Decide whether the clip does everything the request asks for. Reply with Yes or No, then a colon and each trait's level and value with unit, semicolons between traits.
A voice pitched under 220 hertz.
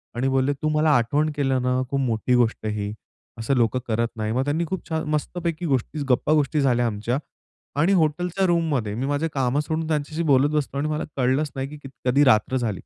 Yes: medium, 140 Hz